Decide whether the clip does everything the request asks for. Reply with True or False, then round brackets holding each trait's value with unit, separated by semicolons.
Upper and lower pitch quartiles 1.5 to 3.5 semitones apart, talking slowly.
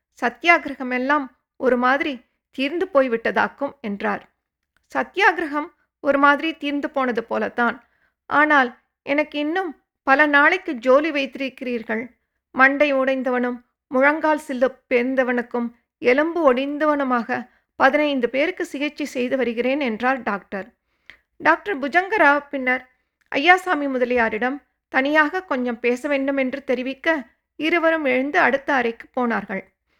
True (3.1 semitones; 100 wpm)